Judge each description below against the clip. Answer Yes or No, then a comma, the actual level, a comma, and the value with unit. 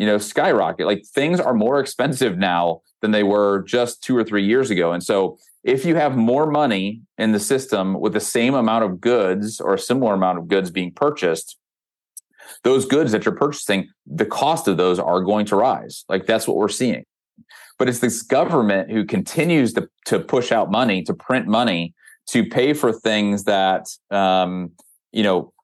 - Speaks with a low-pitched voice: Yes, low, 105 Hz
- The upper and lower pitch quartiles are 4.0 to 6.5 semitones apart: Yes, average, 4.4 semitones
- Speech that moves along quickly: No, average, 190 wpm